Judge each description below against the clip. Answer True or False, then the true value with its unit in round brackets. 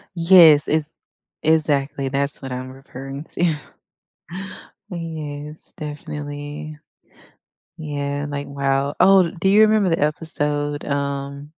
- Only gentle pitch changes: True (2.1 semitones)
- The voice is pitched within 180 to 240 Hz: False (145 Hz)